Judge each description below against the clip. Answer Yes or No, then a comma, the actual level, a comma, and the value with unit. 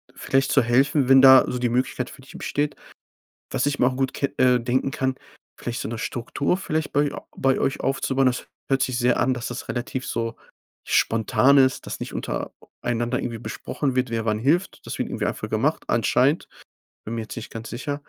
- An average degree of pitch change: No, narrow, 2.1 semitones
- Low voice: Yes, low, 130 Hz